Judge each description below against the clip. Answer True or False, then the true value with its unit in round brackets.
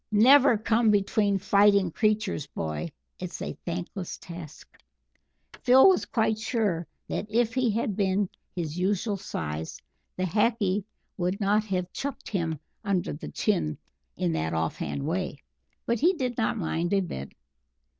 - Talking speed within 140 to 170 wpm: True (145 wpm)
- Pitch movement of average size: True (4.3 semitones)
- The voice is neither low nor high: False (200 Hz)